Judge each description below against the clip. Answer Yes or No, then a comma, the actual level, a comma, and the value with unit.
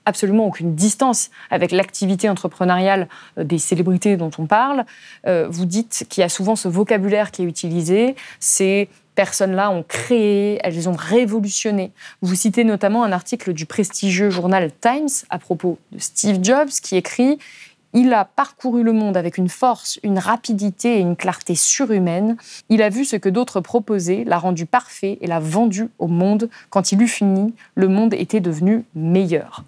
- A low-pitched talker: No, high, 200 Hz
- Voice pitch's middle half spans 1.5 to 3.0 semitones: No, average, 3.4 semitones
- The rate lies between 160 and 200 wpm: Yes, average, 170 wpm